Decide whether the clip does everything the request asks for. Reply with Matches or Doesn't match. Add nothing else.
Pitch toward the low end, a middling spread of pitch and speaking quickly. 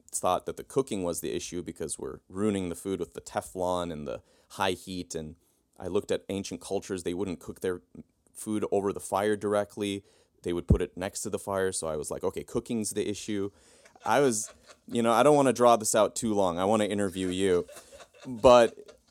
Matches